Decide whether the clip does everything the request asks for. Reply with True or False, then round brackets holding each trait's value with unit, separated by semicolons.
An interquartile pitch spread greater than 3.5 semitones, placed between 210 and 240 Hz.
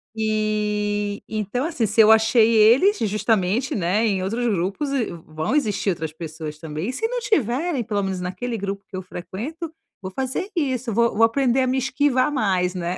True (5.1 semitones; 215 Hz)